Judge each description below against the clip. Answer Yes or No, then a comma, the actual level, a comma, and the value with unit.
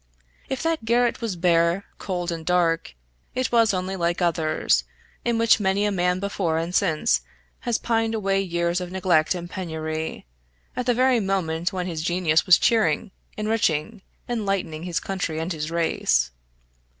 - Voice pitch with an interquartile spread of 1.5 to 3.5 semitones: No, average, 4.2 semitones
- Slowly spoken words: No, average, 160 wpm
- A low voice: No, medium, 180 Hz